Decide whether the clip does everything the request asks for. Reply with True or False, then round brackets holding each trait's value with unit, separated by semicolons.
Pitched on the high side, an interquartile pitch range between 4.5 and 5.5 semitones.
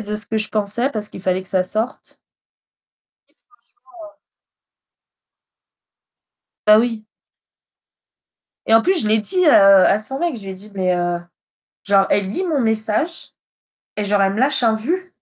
True (215 Hz; 5.1 semitones)